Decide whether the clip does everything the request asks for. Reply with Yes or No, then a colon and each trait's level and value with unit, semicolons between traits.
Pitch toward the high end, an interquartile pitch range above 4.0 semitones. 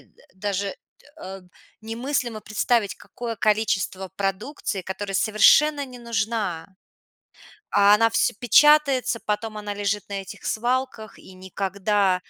No: high, 210 Hz; average, 3.2 semitones